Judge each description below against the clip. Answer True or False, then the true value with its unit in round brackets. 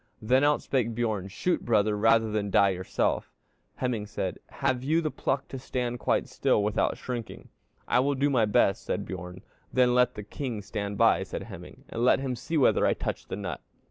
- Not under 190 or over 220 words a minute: True (200 wpm)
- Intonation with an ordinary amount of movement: True (3.9 semitones)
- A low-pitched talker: True (115 Hz)